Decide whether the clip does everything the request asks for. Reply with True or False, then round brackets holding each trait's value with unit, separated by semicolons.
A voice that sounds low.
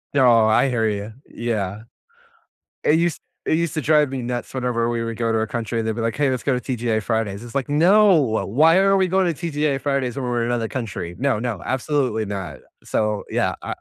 True (120 Hz)